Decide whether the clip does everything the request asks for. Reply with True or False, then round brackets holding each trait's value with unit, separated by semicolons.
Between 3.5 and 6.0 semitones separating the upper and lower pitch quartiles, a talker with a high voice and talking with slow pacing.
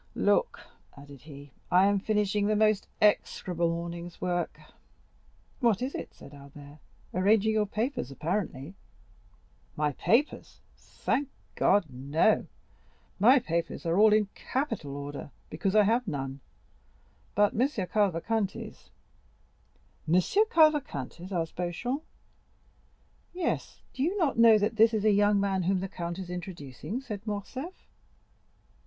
True (4.7 semitones; 195 Hz; 125 wpm)